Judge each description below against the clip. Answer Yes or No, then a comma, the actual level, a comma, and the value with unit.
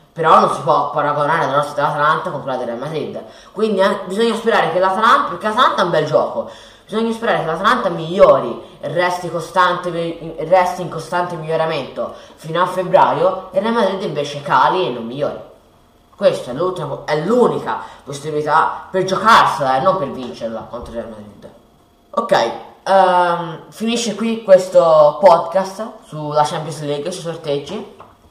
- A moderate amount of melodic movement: Yes, average, 4.5 semitones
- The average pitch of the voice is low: No, medium, 175 Hz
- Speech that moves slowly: No, average, 155 wpm